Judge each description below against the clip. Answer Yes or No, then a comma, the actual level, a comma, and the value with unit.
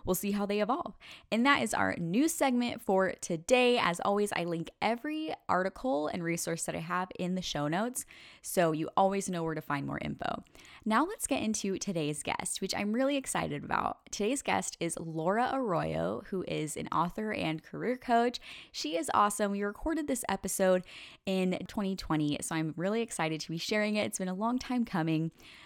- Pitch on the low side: No, high, 195 Hz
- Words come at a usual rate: Yes, average, 195 wpm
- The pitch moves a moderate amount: No, wide, 5.7 semitones